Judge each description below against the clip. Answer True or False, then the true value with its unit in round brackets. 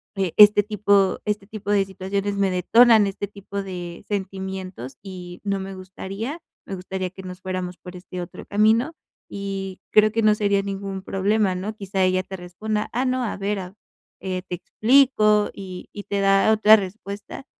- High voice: True (195 Hz)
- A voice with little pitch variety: True (2.0 semitones)